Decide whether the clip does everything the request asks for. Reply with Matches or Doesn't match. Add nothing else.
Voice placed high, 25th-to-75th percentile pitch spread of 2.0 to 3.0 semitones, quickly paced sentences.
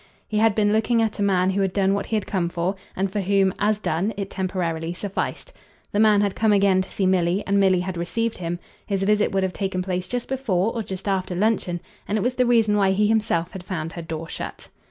Matches